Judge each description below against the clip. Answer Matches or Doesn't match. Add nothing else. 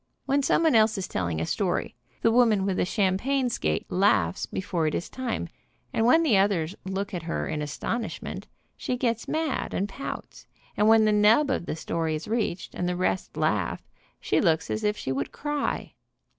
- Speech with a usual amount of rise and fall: Doesn't match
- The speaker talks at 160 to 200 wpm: Matches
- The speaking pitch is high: Matches